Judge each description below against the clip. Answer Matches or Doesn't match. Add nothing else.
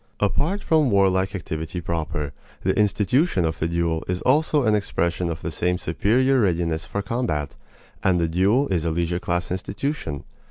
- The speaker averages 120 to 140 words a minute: Doesn't match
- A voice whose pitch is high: Doesn't match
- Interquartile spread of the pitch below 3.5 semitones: Doesn't match